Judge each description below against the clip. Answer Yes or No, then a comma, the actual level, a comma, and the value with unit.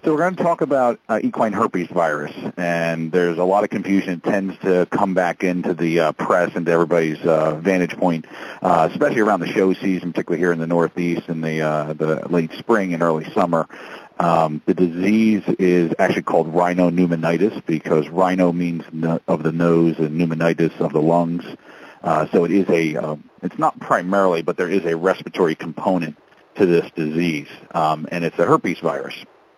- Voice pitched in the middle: No, very low, 85 Hz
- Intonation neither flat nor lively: No, narrow, 1.9 semitones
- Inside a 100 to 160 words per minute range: No, average, 190 wpm